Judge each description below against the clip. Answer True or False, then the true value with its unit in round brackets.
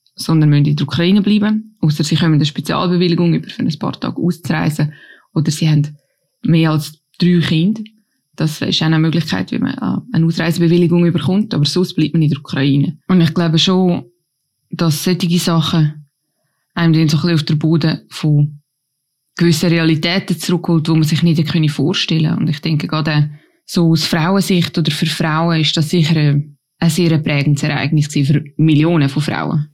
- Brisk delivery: False (170 wpm)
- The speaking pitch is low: False (160 Hz)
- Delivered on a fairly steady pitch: True (2.2 semitones)